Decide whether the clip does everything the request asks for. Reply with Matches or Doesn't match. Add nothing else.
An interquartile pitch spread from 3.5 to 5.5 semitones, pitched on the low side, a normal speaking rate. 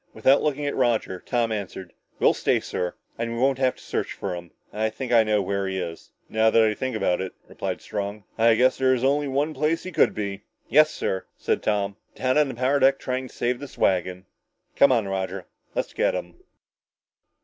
Doesn't match